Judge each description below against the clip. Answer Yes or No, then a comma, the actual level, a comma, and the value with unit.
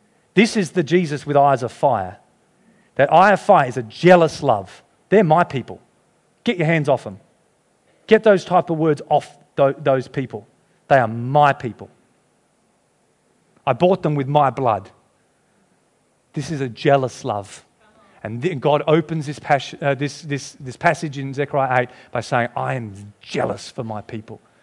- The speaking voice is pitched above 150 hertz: No, medium, 140 Hz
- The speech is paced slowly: No, average, 165 wpm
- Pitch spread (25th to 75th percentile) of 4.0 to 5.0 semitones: Yes, average, 4.4 semitones